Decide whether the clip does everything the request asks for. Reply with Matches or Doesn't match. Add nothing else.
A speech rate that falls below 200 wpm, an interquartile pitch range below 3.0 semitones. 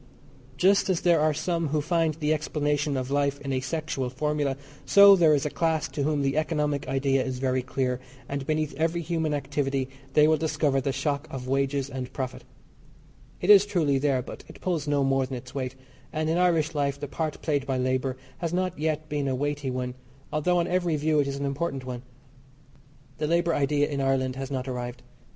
Doesn't match